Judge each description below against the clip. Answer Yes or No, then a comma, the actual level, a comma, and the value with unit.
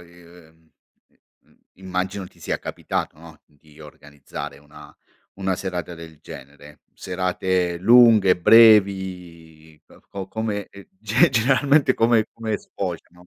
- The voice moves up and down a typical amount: Yes, average, 4.3 semitones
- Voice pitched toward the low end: Yes, very low, 90 Hz